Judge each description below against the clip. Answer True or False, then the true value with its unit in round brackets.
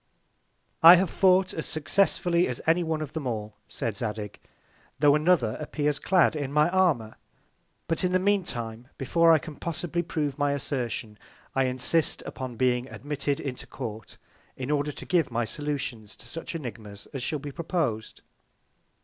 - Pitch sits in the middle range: True (145 Hz)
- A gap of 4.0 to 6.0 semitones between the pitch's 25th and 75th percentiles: True (5.3 semitones)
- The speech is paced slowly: False (165 wpm)